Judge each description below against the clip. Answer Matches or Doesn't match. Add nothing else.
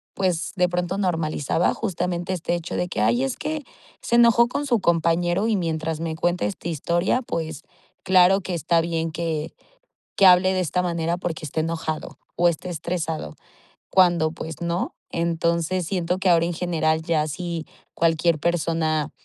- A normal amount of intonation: Doesn't match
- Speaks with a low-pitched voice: Doesn't match